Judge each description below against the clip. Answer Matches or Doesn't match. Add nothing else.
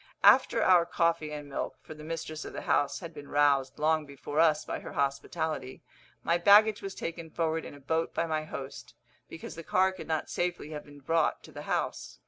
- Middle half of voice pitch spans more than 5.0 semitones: Doesn't match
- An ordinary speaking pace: Doesn't match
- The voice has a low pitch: Doesn't match